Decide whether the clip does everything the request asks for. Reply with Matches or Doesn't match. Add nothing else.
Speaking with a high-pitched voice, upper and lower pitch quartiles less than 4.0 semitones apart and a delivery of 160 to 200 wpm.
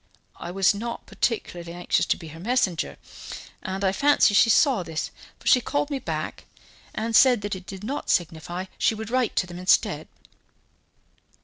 Doesn't match